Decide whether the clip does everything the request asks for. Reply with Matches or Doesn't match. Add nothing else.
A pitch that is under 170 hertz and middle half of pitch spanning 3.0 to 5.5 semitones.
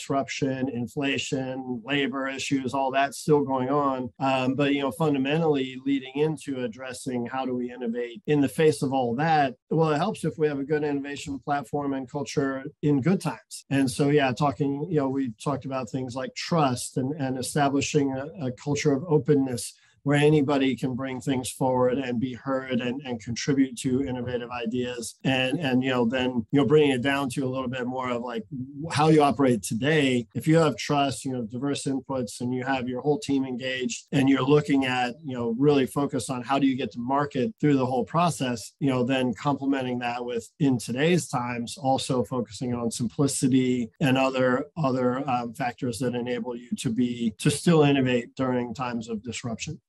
Doesn't match